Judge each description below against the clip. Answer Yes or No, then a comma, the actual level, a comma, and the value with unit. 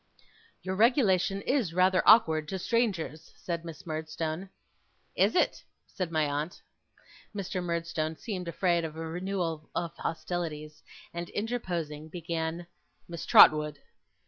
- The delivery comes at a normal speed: No, slow, 120 wpm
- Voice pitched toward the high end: No, medium, 170 Hz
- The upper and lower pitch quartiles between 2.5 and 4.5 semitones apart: Yes, average, 2.9 semitones